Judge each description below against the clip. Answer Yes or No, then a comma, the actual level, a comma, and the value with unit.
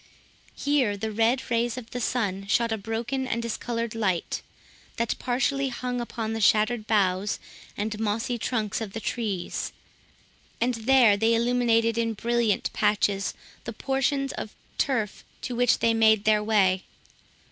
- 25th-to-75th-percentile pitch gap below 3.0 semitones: Yes, narrow, 2.4 semitones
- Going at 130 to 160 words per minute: Yes, average, 145 wpm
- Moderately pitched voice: No, high, 225 Hz